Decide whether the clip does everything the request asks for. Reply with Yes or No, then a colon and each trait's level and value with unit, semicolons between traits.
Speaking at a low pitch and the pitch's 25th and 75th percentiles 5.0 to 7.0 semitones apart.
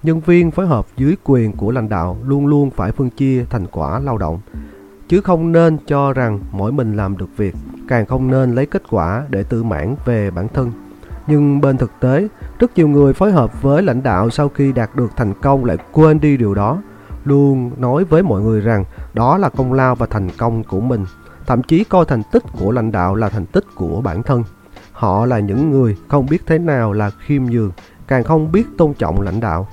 Yes: low, 125 Hz; wide, 5.5 semitones